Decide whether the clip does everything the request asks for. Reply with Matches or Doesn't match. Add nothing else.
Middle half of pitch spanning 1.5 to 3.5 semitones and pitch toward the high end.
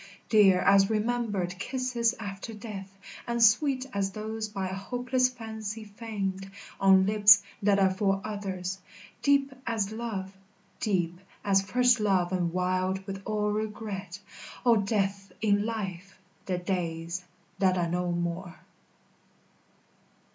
Matches